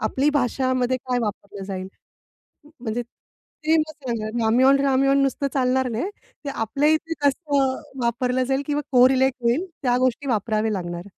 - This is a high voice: Yes, very high, 255 Hz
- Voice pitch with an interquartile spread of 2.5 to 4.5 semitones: Yes, average, 3.3 semitones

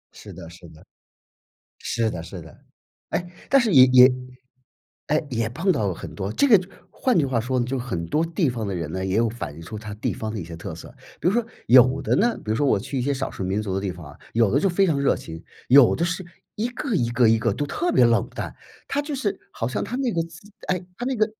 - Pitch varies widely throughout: Yes, wide, 9.0 semitones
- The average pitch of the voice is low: Yes, low, 125 Hz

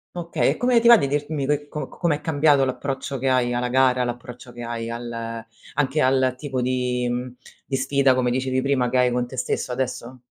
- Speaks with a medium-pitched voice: No, low, 130 Hz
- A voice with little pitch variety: Yes, narrow, 2.3 semitones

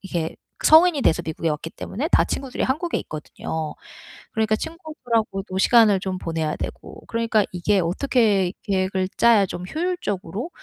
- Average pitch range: No, wide, 5.9 semitones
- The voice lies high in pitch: Yes, high, 205 Hz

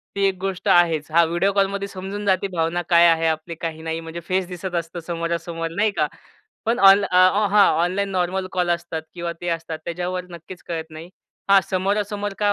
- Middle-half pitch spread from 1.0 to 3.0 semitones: Yes, average, 2.7 semitones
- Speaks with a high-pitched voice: No, medium, 175 Hz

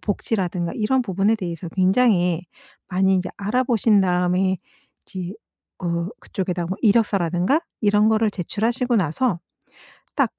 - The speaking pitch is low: No, high, 190 Hz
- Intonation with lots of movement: No, average, 3.6 semitones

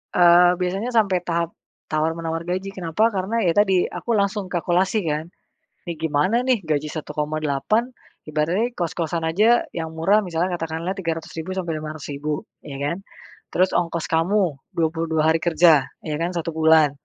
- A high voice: No, medium, 165 Hz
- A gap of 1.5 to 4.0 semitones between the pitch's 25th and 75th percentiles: Yes, average, 2.7 semitones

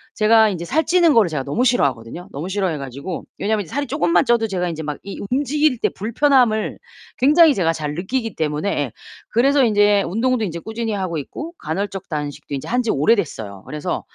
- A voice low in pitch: No, high, 200 Hz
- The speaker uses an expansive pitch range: Yes, wide, 7.1 semitones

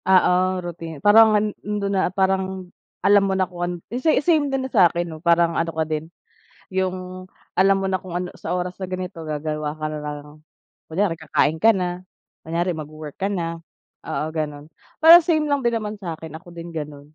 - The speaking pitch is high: No, medium, 180 Hz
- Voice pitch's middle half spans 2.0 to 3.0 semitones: No, average, 3.4 semitones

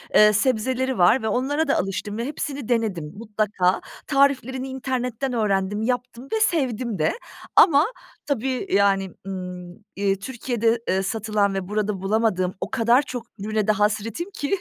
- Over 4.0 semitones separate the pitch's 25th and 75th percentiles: Yes, average, 4.6 semitones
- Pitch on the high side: Yes, high, 225 Hz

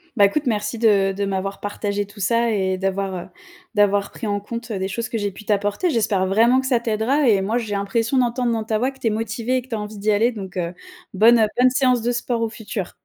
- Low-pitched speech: No, high, 215 Hz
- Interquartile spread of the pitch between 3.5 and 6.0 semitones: No, average, 2.8 semitones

